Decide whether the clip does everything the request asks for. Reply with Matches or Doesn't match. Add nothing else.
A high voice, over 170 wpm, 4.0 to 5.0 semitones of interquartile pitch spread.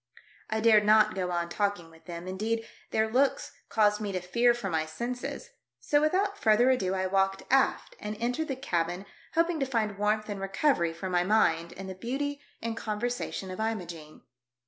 Matches